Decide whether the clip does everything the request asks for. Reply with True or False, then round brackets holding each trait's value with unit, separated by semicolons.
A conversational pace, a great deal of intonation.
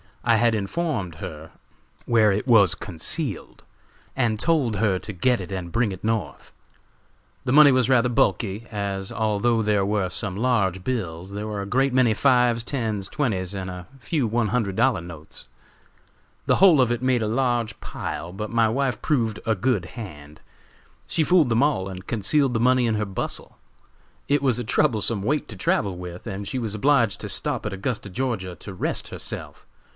False (180 wpm; 4.4 semitones)